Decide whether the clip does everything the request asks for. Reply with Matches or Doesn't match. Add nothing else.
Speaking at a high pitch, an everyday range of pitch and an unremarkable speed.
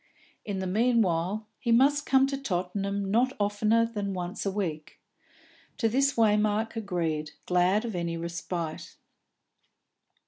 Doesn't match